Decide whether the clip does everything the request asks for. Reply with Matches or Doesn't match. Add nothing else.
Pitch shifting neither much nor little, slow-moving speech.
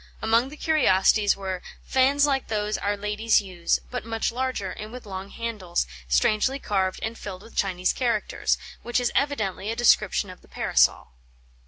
Doesn't match